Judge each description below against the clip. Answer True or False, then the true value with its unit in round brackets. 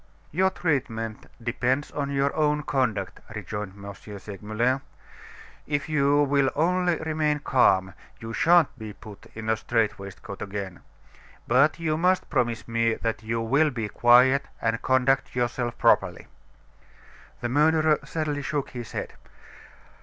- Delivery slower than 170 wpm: True (135 wpm)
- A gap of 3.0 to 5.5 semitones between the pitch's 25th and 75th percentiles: True (4.9 semitones)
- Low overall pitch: True (125 Hz)